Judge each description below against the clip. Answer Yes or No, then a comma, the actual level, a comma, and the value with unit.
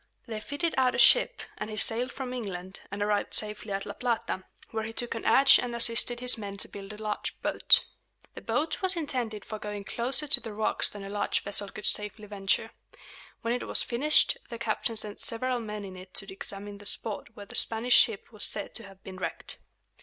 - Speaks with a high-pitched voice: Yes, high, 215 Hz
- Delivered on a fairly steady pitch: No, average, 3.0 semitones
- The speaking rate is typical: No, fast, 215 wpm